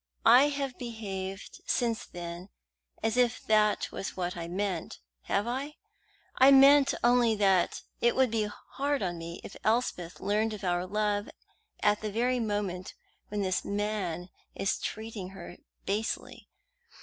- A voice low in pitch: No, high, 210 Hz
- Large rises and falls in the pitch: No, average, 4.1 semitones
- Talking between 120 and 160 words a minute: Yes, average, 145 wpm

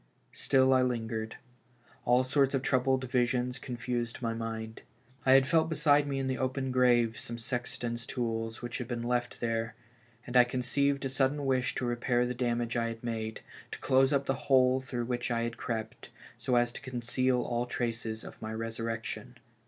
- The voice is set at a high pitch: No, low, 125 Hz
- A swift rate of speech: No, average, 185 wpm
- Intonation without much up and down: Yes, narrow, 2.0 semitones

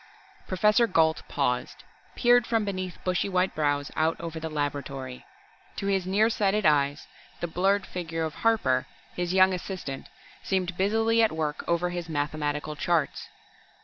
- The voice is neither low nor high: Yes, medium, 175 Hz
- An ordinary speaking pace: Yes, average, 145 wpm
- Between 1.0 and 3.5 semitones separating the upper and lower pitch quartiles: No, average, 4.4 semitones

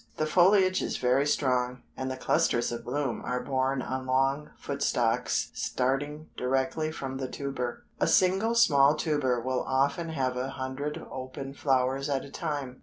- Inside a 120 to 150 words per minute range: No, average, 165 wpm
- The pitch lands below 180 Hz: Yes, low, 135 Hz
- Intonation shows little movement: Yes, narrow, 2.3 semitones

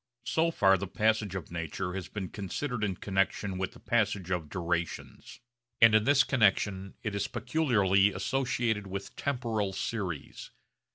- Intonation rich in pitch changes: No, average, 3.4 semitones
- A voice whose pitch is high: No, low, 100 Hz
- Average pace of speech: Yes, average, 150 wpm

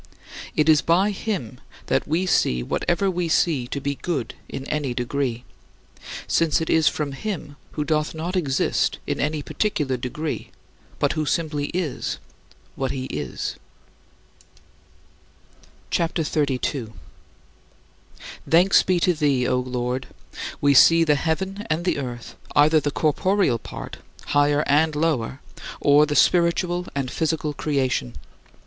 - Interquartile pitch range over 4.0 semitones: No, average, 3.7 semitones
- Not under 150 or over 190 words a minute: No, average, 140 wpm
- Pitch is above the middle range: No, medium, 150 Hz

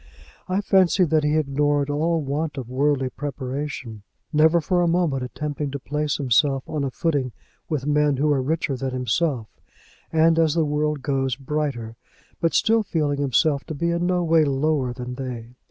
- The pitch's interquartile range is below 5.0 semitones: Yes, average, 3.0 semitones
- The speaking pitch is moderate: Yes, medium, 145 Hz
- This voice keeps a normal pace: Yes, average, 175 wpm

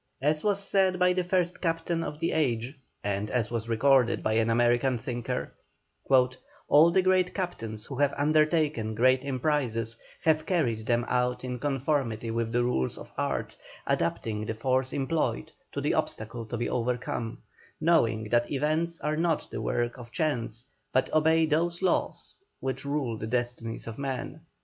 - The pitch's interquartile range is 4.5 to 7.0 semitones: Yes, average, 5.1 semitones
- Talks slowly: No, average, 165 wpm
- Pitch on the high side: No, low, 130 Hz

